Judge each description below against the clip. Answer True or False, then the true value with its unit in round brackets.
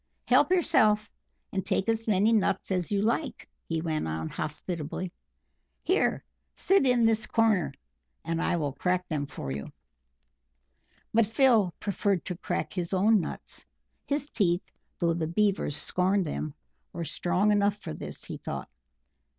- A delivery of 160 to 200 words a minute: False (150 wpm)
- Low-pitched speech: False (190 Hz)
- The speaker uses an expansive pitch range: False (4.5 semitones)